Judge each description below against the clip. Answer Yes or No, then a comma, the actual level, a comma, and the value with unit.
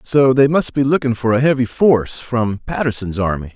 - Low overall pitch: Yes, low, 125 Hz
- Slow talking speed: No, average, 200 wpm